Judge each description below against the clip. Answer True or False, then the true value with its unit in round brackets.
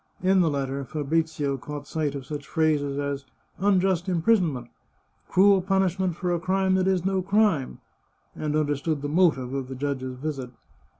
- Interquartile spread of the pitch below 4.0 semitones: False (4.9 semitones)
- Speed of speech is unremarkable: True (175 wpm)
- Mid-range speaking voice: True (155 Hz)